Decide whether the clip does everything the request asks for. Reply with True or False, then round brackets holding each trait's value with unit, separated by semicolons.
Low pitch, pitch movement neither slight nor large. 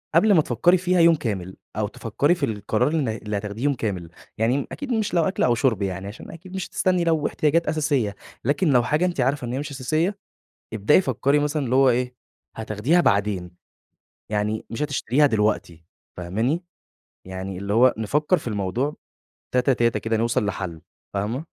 False (125 Hz; 6.4 semitones)